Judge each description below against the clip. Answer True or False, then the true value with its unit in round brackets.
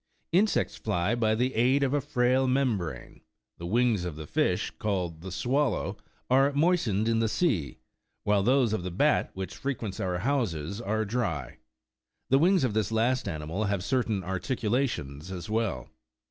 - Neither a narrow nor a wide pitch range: False (5.8 semitones)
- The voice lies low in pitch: True (110 Hz)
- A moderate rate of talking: True (160 wpm)